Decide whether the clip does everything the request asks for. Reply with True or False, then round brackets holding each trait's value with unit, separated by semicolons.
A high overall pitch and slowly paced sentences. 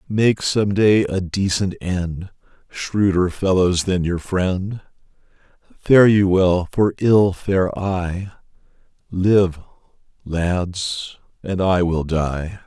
False (95 Hz; 115 wpm)